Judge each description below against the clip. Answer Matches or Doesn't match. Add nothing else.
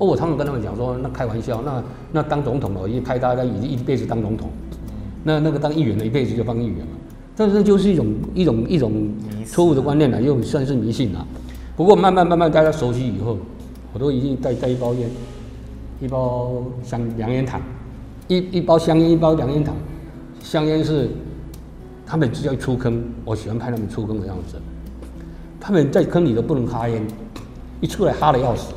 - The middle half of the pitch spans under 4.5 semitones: Doesn't match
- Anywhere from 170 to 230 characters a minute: Doesn't match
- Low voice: Matches